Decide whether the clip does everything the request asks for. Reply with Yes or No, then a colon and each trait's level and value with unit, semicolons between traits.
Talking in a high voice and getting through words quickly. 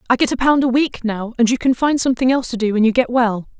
Yes: high, 245 Hz; fast, 315 wpm